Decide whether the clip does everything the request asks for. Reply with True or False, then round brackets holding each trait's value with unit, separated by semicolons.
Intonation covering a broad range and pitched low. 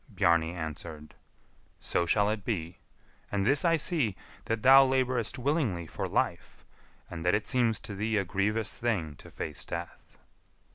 True (6.2 semitones; 105 Hz)